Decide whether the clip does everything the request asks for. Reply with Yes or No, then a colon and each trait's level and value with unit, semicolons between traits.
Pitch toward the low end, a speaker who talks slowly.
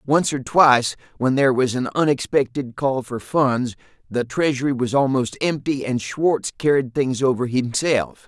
No: low, 130 Hz; average, 160 wpm